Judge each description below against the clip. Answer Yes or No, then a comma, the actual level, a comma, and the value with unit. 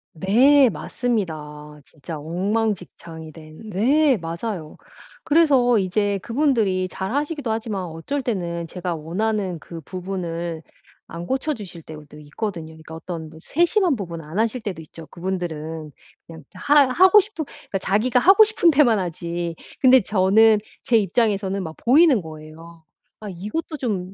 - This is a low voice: No, high, 190 Hz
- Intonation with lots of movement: Yes, wide, 6.7 semitones